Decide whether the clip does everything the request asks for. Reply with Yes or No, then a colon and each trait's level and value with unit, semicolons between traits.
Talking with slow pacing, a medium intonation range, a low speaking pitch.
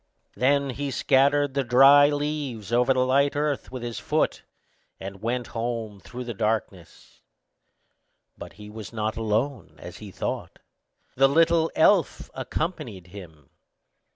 Yes: slow, 130 wpm; average, 4.7 semitones; low, 125 Hz